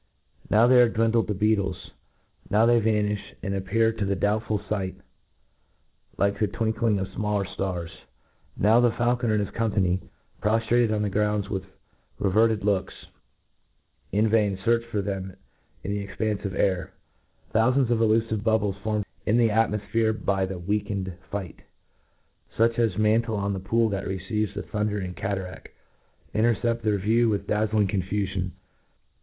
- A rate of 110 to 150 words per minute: No, average, 160 wpm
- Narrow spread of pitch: Yes, narrow, 2.3 semitones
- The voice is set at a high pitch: No, low, 105 Hz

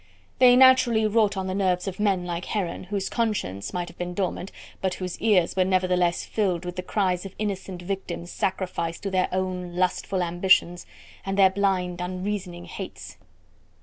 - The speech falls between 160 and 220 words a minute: Yes, average, 170 wpm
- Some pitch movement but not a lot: No, narrow, 1.9 semitones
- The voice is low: No, medium, 185 Hz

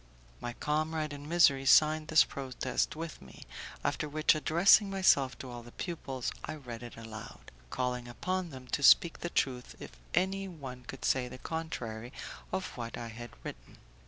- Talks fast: No, average, 170 wpm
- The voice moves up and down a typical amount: Yes, average, 4.7 semitones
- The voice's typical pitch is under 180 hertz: Yes, medium, 140 Hz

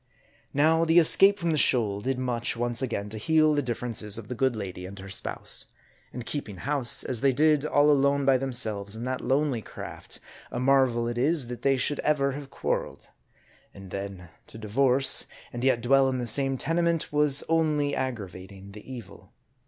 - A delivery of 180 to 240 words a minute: Yes, average, 190 wpm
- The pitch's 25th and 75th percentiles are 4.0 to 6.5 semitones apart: Yes, average, 4.3 semitones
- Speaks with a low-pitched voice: Yes, low, 130 Hz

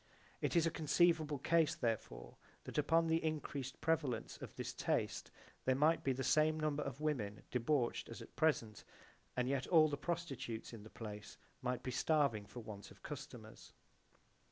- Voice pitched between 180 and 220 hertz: No, medium, 140 Hz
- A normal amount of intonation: Yes, average, 4.8 semitones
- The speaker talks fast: No, average, 170 wpm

